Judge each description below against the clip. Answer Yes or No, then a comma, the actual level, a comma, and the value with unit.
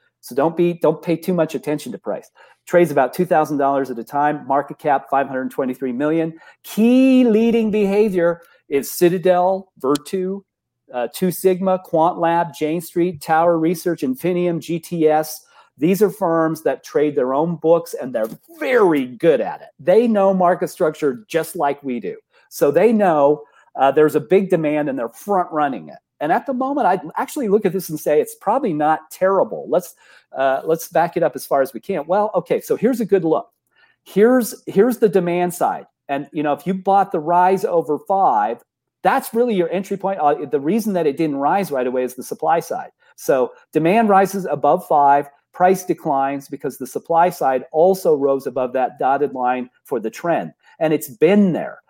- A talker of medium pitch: Yes, medium, 170 Hz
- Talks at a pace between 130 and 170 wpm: No, average, 195 wpm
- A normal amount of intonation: Yes, average, 4.8 semitones